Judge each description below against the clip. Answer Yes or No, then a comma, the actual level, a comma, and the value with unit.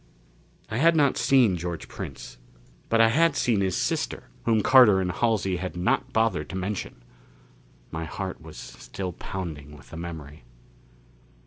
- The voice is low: Yes, very low, 95 Hz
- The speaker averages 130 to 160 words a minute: Yes, average, 150 wpm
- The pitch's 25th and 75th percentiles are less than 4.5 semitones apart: No, average, 5.0 semitones